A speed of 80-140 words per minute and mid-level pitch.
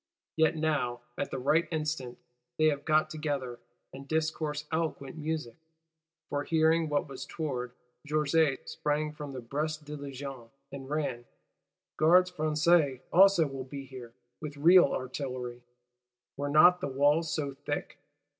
Yes: slow, 135 wpm; medium, 150 Hz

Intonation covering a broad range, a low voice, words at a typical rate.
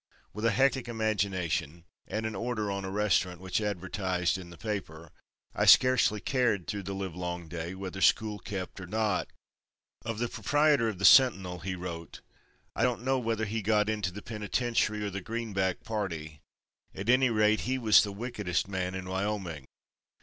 No: average, 3.4 semitones; low, 100 Hz; average, 170 wpm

